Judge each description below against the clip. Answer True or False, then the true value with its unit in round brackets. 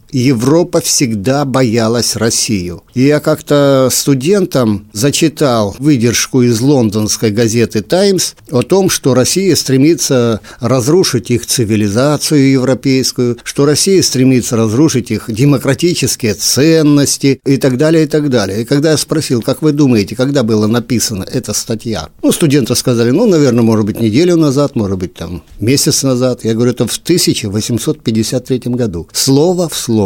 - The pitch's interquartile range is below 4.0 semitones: False (4.3 semitones)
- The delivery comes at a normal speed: True (140 wpm)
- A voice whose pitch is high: False (130 Hz)